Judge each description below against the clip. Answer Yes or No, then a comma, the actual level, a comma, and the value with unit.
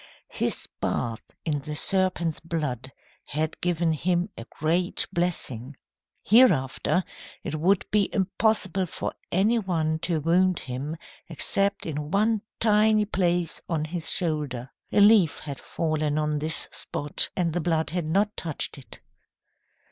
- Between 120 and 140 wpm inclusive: Yes, slow, 135 wpm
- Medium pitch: Yes, medium, 165 Hz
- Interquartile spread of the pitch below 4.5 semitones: Yes, average, 3.7 semitones